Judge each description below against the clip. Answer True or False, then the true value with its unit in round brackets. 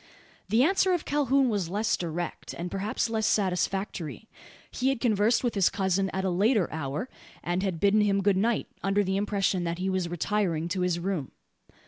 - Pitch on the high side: True (195 Hz)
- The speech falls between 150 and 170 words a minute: False (185 wpm)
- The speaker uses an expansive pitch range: False (3.5 semitones)